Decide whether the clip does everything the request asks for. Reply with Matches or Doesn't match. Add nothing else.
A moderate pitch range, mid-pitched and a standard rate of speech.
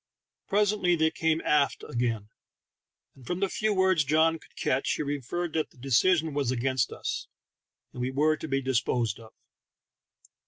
Matches